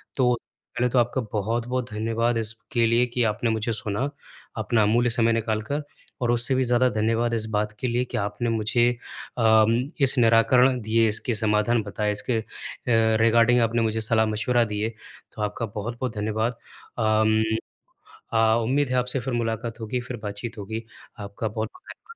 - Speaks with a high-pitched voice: No, low, 115 Hz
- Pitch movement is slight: Yes, narrow, 1.9 semitones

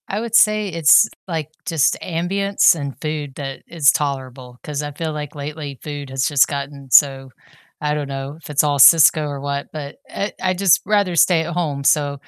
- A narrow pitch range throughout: No, average, 3.1 semitones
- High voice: No, medium, 150 Hz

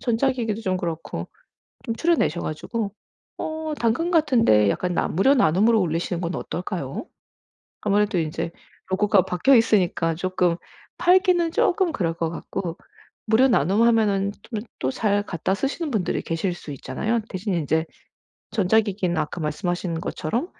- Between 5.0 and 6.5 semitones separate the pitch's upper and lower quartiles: Yes, wide, 5.4 semitones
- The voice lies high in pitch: Yes, high, 200 Hz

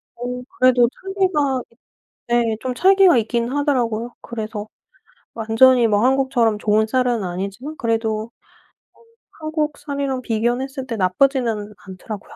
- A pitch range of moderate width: Yes, average, 3.4 semitones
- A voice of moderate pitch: No, high, 240 Hz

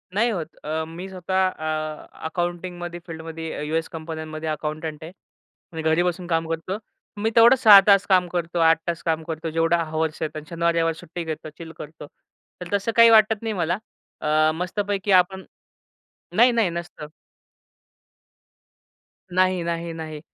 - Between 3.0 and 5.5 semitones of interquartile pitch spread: No, narrow, 2.6 semitones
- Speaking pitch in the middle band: Yes, medium, 170 Hz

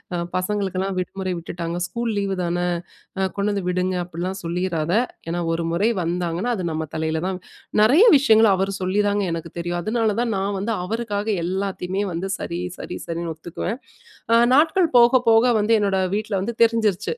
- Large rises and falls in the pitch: No, average, 3.7 semitones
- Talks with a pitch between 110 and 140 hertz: No, high, 190 Hz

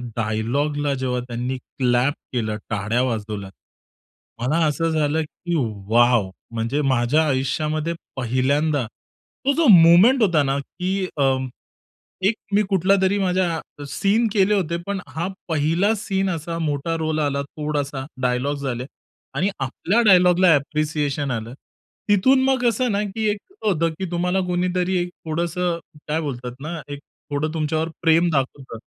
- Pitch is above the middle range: No, medium, 155 Hz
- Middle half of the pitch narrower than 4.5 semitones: No, average, 5.1 semitones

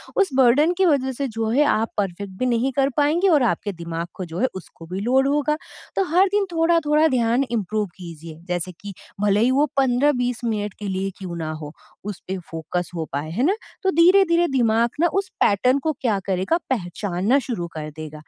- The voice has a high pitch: Yes, high, 230 Hz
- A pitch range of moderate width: No, wide, 7.6 semitones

